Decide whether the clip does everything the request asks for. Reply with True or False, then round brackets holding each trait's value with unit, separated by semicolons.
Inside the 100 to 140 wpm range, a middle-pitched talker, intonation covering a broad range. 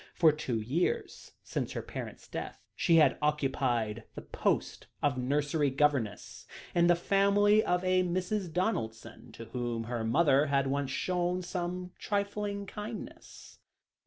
True (135 wpm; 155 Hz; 6.0 semitones)